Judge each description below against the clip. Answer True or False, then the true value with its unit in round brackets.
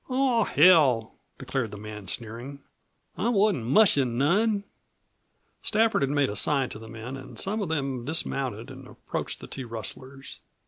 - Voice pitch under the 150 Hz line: True (135 Hz)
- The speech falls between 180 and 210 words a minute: False (155 wpm)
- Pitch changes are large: True (8.3 semitones)